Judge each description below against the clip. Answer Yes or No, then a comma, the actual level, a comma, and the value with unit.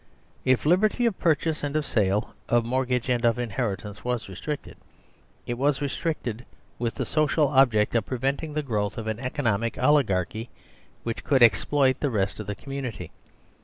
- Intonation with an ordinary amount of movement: Yes, average, 4.6 semitones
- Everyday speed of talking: Yes, average, 165 wpm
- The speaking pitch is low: Yes, low, 125 Hz